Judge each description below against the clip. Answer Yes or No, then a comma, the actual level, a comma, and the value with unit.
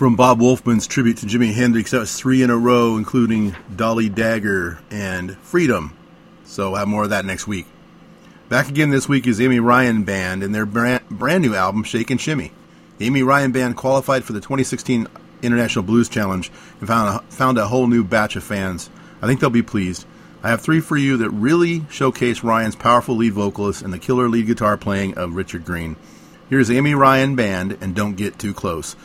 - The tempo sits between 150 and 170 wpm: No, fast, 205 wpm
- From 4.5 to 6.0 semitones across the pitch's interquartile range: No, average, 4.1 semitones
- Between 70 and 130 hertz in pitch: Yes, low, 115 Hz